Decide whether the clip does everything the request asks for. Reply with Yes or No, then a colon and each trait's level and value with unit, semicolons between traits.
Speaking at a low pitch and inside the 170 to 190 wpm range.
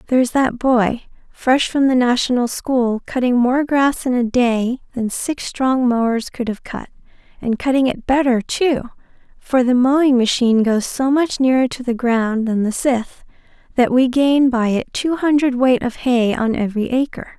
No: very high, 250 Hz; average, 185 wpm